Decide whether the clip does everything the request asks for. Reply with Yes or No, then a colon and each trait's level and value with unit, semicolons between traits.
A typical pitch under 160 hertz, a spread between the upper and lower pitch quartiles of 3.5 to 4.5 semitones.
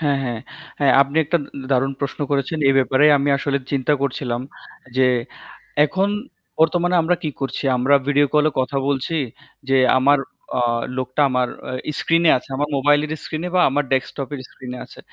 No: medium, 140 Hz; narrow, 2.4 semitones